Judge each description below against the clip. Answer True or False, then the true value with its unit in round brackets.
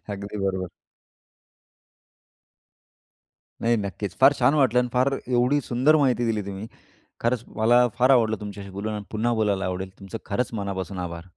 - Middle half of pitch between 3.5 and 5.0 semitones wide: True (3.9 semitones)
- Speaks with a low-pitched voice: True (110 Hz)